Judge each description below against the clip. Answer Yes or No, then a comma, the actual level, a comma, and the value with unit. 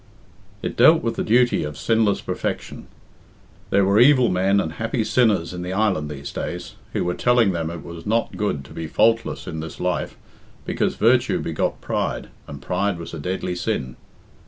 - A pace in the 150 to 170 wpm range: No, average, 180 wpm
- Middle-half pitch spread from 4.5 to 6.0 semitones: Yes, average, 5.3 semitones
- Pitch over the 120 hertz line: No, very low, 95 Hz